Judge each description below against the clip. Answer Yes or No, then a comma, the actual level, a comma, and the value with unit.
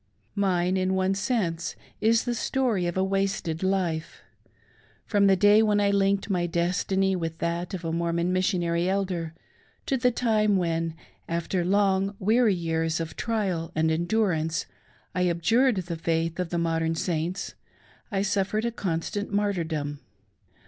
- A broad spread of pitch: No, average, 3.2 semitones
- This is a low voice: No, medium, 185 Hz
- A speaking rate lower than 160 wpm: Yes, average, 150 wpm